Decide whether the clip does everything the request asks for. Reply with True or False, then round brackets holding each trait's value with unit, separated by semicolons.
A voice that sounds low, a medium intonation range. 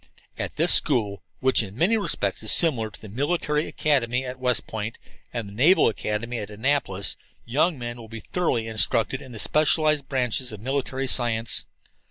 True (125 Hz; 4.2 semitones)